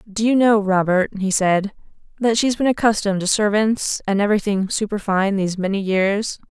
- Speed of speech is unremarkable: Yes, average, 165 wpm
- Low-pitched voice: No, high, 205 Hz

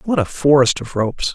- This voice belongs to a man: Yes, male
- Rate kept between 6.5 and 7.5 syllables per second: No, 5.6 syllables/s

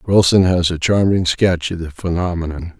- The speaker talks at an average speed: Yes, average, 170 wpm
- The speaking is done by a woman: No, male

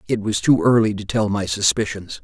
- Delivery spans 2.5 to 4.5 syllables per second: No, 5.3 syllables/s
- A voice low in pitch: Yes, low, 105 Hz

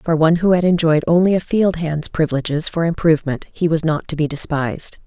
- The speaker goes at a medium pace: No, fast, 215 wpm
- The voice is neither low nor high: Yes, medium, 160 Hz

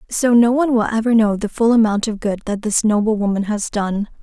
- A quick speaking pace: Yes, fast, 240 wpm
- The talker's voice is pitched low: No, high, 220 Hz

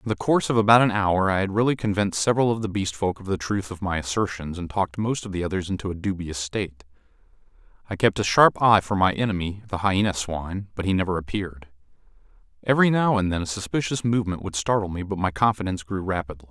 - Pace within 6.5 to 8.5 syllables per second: Yes, 6.6 syllables/s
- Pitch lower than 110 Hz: Yes, low, 100 Hz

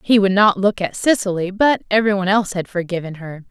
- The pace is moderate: No, fast, 220 wpm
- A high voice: Yes, high, 195 Hz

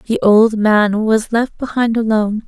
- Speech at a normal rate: Yes, average, 170 wpm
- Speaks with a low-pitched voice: No, high, 220 Hz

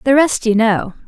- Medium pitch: No, high, 235 Hz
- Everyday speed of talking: No, fast, 225 wpm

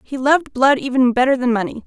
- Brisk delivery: Yes, fast, 225 wpm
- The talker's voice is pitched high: Yes, very high, 255 Hz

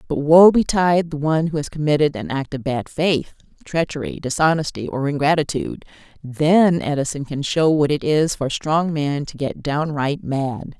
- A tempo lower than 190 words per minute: Yes, average, 180 wpm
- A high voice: No, medium, 150 Hz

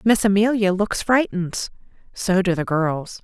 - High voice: Yes, high, 195 Hz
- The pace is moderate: Yes, average, 150 wpm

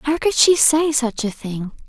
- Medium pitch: No, very high, 270 Hz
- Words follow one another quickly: Yes, fast, 225 wpm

